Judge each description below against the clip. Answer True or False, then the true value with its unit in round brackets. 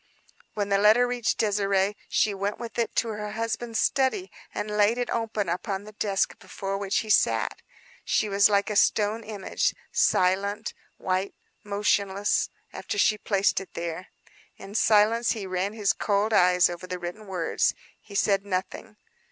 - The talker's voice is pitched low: False (205 Hz)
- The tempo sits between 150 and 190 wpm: True (160 wpm)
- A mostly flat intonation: True (1.9 semitones)